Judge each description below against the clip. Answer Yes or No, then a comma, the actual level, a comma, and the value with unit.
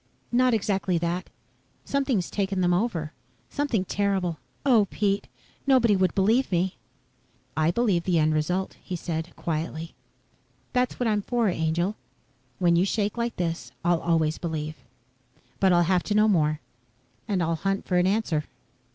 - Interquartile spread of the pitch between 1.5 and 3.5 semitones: No, average, 4.0 semitones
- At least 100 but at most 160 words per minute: Yes, average, 150 wpm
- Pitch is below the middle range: No, medium, 185 Hz